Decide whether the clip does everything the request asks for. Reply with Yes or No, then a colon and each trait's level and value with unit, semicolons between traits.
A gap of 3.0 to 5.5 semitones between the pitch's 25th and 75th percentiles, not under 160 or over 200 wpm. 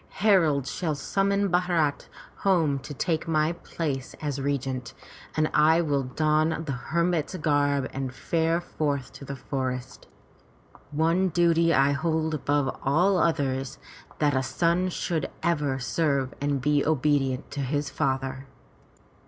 No: average, 3.4 semitones; slow, 135 wpm